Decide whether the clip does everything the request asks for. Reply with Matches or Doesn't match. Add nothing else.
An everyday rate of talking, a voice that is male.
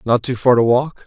Doesn't match